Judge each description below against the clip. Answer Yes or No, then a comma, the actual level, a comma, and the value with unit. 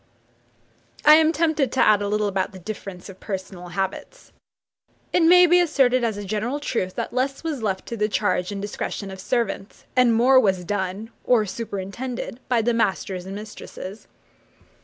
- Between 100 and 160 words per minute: No, average, 175 wpm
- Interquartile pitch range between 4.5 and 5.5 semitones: Yes, average, 4.8 semitones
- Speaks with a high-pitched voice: Yes, high, 215 Hz